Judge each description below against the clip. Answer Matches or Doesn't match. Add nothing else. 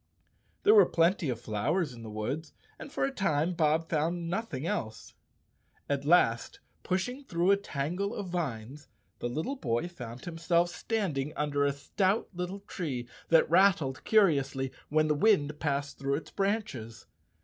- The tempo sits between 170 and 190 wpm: Doesn't match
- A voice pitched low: Doesn't match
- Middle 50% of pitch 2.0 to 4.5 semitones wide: Doesn't match